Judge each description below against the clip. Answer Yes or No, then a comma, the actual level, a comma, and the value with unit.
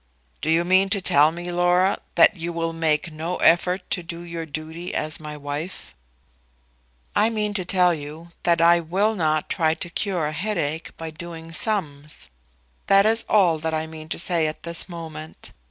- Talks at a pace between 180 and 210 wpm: Yes, average, 185 wpm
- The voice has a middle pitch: Yes, medium, 170 Hz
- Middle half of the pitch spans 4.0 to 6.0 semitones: No, narrow, 2.4 semitones